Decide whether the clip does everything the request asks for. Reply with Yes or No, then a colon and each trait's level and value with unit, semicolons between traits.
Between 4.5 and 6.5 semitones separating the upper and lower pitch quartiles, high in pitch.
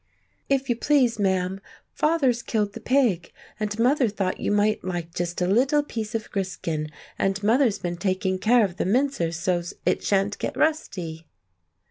Yes: average, 4.9 semitones; high, 205 Hz